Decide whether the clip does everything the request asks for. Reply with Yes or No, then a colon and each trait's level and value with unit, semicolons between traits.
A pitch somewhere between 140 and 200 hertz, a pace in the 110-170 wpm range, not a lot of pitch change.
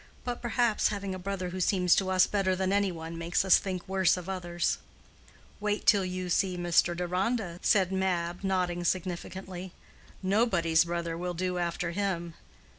Yes: medium, 185 Hz; average, 165 wpm; narrow, 1.8 semitones